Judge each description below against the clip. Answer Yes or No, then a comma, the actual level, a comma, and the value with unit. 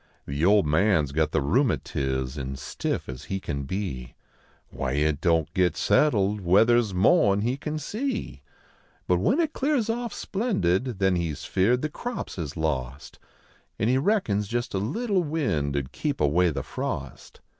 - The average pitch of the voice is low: Yes, very low, 95 Hz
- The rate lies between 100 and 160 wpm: No, average, 180 wpm